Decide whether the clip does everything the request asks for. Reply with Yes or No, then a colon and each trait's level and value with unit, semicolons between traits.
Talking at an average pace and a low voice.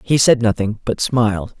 Yes: average, 190 wpm; low, 115 Hz